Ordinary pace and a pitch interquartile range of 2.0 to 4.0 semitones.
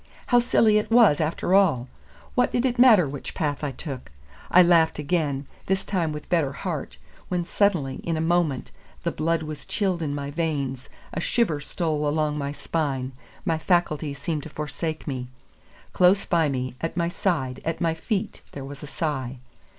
Yes: average, 180 wpm; average, 3.7 semitones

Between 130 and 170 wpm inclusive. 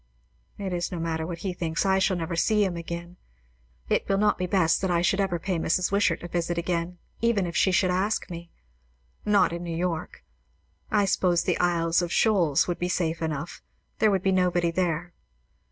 No: average, 200 wpm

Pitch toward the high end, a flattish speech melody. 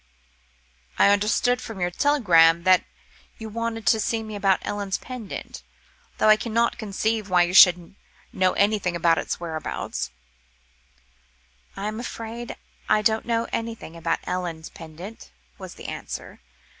No: high, 205 Hz; average, 4.1 semitones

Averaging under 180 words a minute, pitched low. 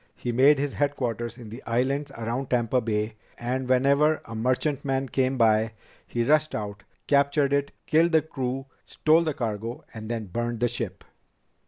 Yes: average, 165 wpm; low, 125 Hz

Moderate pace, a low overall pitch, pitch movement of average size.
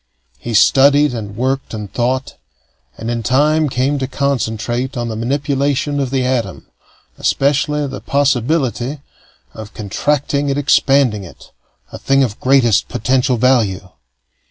No: slow, 130 wpm; low, 130 Hz; average, 3.1 semitones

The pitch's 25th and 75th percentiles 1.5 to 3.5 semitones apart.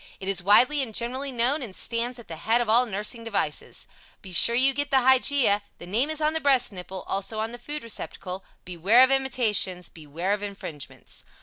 No: average, 5.2 semitones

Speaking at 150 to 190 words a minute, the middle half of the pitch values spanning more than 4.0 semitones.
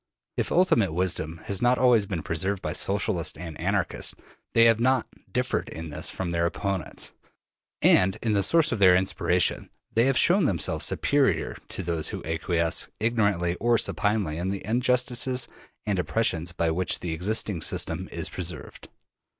Yes: average, 160 wpm; average, 5.2 semitones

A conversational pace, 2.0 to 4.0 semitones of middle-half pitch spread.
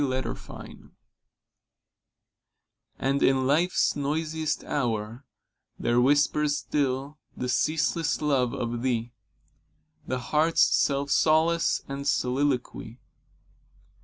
No: slow, 90 wpm; average, 3.1 semitones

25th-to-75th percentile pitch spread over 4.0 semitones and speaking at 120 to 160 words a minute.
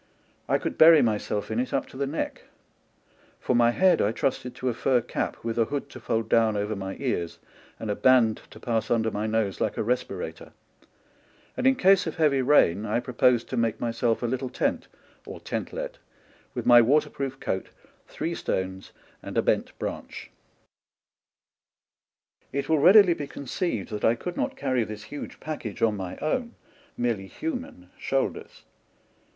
No: average, 4.7 semitones; average, 175 wpm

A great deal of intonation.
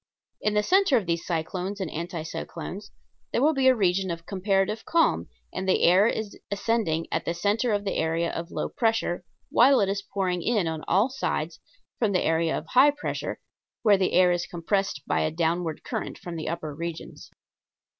No: average, 4.1 semitones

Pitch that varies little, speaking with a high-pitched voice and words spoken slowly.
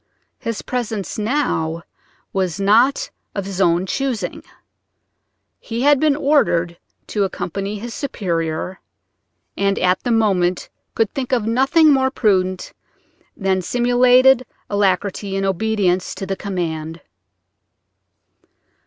No: average, 5.0 semitones; high, 200 Hz; slow, 110 wpm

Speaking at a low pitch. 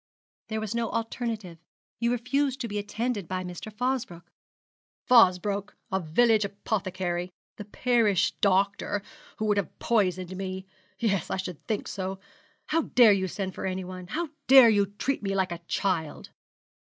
No: high, 200 Hz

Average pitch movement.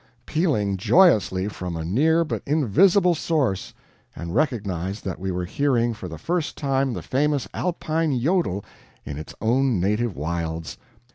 No: wide, 8.6 semitones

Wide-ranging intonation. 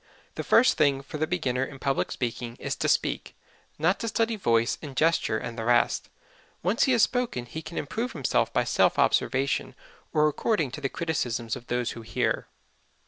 Yes: wide, 6.0 semitones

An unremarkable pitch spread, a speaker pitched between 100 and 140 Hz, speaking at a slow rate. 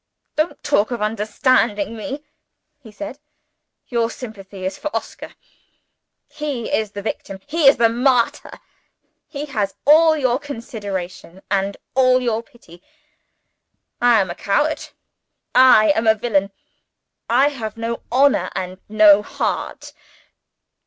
No: average, 4.7 semitones; high, 230 Hz; slow, 125 wpm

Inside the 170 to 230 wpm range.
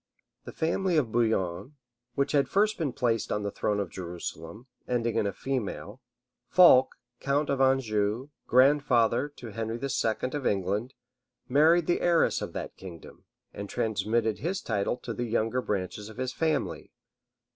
No: average, 155 wpm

